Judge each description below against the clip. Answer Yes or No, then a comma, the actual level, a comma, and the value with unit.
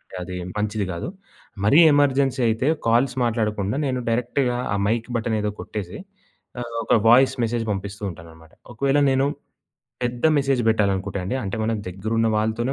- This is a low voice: Yes, low, 115 Hz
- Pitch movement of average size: Yes, average, 3.7 semitones